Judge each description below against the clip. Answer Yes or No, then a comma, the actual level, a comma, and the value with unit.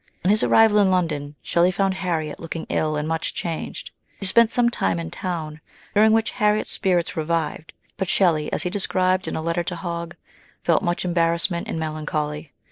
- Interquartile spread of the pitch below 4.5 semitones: Yes, average, 3.2 semitones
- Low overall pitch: No, medium, 170 Hz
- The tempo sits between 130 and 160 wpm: No, average, 185 wpm